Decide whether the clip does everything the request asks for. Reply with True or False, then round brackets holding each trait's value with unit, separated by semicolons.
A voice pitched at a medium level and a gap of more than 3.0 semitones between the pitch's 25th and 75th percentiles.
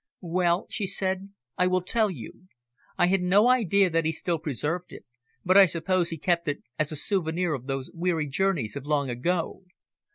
True (175 Hz; 3.5 semitones)